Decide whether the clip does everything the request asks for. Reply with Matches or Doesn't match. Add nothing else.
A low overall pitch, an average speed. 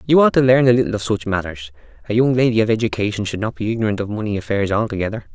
Doesn't match